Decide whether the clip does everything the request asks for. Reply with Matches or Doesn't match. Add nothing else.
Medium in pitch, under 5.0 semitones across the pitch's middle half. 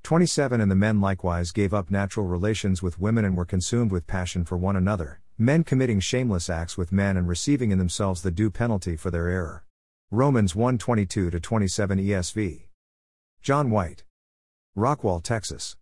Doesn't match